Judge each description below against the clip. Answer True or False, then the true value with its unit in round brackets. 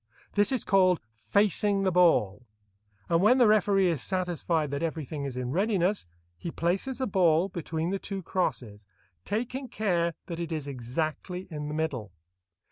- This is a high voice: False (170 Hz)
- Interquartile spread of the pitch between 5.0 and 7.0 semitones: False (4.5 semitones)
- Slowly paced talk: False (160 wpm)